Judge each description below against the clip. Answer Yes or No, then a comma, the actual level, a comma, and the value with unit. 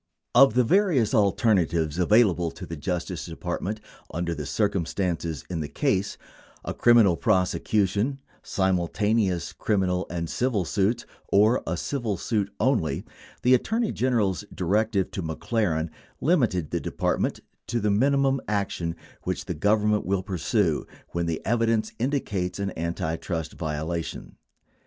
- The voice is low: Yes, low, 100 Hz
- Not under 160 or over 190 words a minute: No, average, 145 wpm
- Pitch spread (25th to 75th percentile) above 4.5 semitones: Yes, average, 4.9 semitones